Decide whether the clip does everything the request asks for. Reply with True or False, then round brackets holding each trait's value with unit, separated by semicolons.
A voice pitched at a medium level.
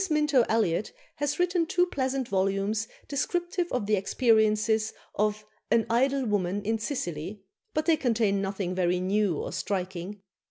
False (215 Hz)